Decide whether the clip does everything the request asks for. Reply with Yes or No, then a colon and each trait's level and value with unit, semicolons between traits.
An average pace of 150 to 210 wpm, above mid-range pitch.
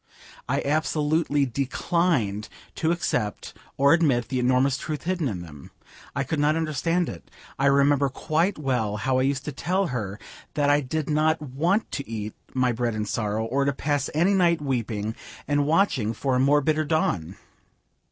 No: average, 170 wpm; medium, 140 Hz